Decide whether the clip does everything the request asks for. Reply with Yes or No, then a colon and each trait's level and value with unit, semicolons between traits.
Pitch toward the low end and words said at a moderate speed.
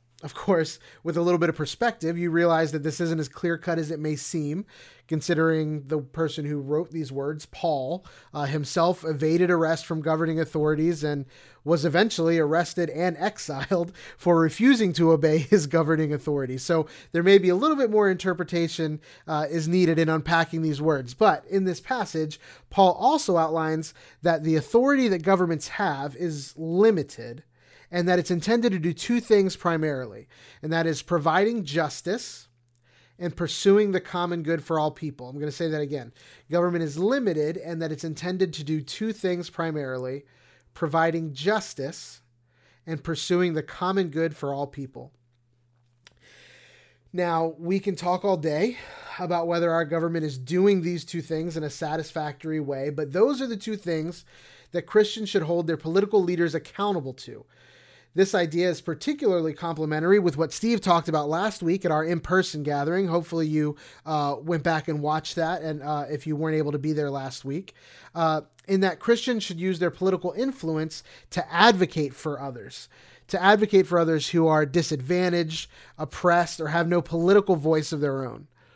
No: medium, 165 Hz; average, 170 wpm